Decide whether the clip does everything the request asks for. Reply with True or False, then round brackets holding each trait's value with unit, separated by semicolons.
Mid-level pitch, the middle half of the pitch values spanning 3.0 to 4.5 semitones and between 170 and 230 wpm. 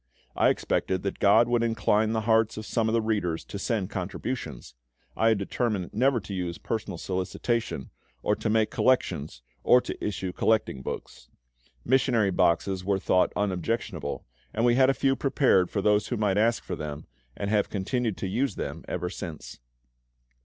False (105 Hz; 3.8 semitones; 175 wpm)